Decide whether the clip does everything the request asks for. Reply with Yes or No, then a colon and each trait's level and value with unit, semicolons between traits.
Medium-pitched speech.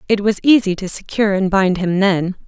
No: high, 195 Hz